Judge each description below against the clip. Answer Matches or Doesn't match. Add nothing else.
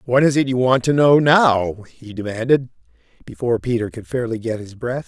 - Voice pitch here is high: Doesn't match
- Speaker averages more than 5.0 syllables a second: Matches